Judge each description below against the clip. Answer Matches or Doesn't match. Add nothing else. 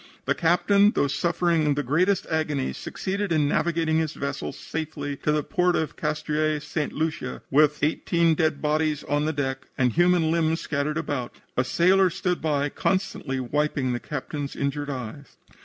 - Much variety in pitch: Doesn't match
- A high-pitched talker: Doesn't match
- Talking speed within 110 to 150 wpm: Doesn't match